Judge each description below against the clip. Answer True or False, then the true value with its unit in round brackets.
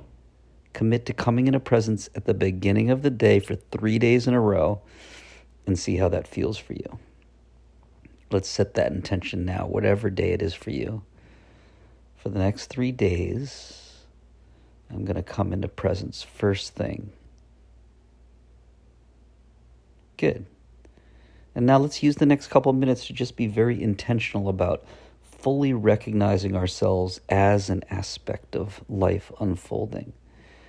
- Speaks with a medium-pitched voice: False (100 Hz)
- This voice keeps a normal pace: True (145 wpm)